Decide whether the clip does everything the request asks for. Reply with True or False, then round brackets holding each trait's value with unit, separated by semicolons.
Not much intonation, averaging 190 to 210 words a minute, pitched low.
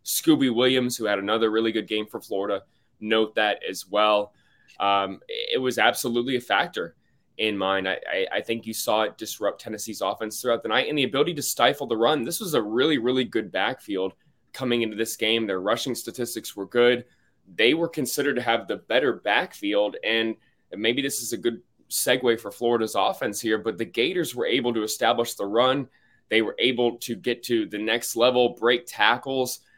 True (2.2 semitones; 195 wpm; 115 Hz)